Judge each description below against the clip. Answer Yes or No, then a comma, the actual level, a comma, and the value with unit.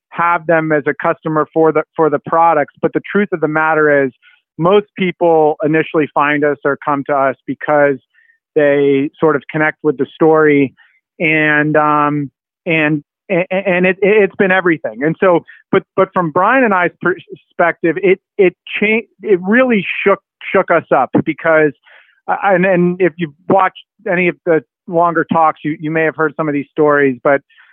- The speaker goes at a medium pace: Yes, average, 175 wpm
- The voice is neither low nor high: Yes, medium, 160 Hz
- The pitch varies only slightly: No, average, 3.6 semitones